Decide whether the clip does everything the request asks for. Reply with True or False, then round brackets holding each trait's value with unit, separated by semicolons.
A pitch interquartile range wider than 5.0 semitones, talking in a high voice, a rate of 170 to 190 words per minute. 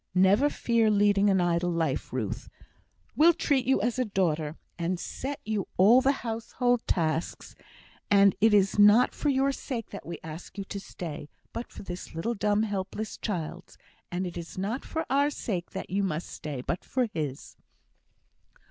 True (5.4 semitones; 200 Hz; 175 wpm)